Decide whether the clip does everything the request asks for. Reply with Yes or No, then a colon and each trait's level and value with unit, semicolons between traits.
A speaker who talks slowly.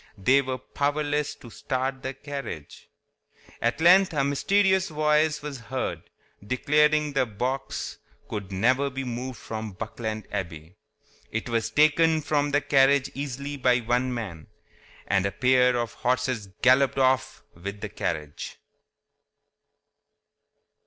Yes: slow, 130 wpm